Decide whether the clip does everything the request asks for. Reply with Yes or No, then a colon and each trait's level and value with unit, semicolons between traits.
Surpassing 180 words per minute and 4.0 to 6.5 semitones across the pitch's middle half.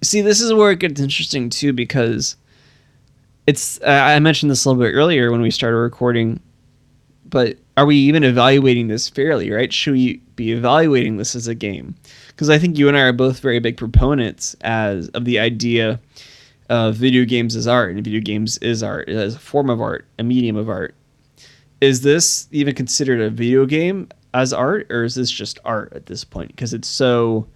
No: average, 195 wpm; average, 3.2 semitones